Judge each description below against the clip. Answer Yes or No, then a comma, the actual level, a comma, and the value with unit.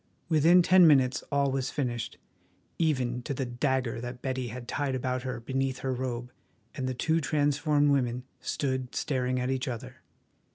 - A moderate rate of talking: Yes, average, 165 wpm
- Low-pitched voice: Yes, low, 130 Hz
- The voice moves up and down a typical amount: No, narrow, 2.3 semitones